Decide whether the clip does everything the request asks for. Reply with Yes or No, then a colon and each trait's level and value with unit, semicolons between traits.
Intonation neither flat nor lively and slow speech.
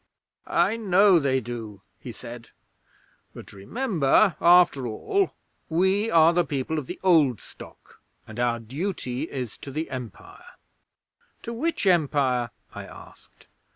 No: wide, 7.1 semitones; slow, 130 wpm